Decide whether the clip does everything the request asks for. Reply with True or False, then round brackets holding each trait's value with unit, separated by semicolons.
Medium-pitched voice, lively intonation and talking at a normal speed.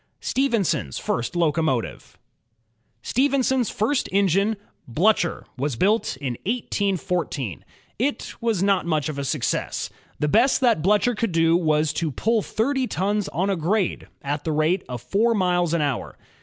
True (180 Hz; 6.2 semitones; 145 wpm)